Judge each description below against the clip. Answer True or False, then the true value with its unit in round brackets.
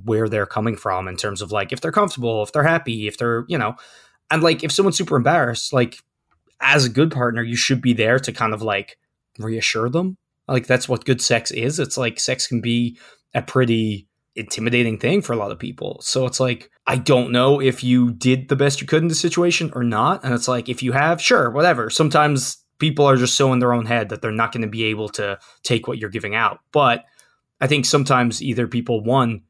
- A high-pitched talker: False (125 Hz)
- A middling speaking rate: False (230 wpm)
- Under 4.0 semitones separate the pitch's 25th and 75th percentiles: True (3.3 semitones)